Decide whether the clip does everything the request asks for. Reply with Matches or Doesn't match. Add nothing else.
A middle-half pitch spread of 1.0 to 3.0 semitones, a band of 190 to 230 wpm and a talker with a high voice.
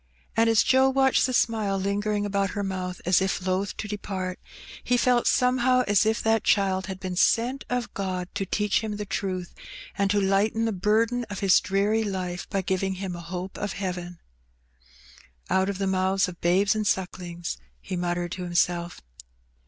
Matches